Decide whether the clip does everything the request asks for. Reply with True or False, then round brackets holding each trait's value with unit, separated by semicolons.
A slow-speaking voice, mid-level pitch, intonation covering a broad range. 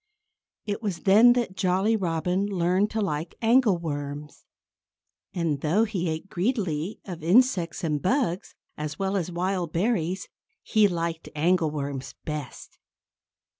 False (125 wpm; 180 Hz; 4.2 semitones)